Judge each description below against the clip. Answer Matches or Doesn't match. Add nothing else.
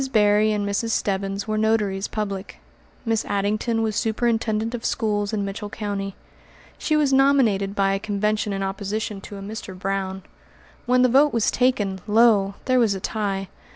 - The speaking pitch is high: Matches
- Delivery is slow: Doesn't match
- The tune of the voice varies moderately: Doesn't match